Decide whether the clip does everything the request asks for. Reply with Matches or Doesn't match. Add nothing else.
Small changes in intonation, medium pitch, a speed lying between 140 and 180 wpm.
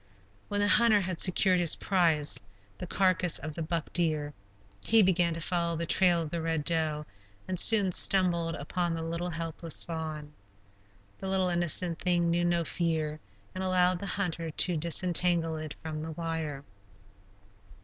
Matches